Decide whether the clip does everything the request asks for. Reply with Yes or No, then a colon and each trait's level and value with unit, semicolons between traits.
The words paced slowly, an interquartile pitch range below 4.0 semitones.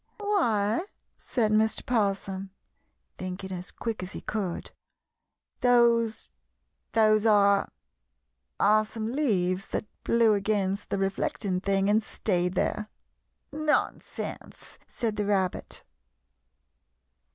Yes: slow, 105 wpm; narrow, 2.6 semitones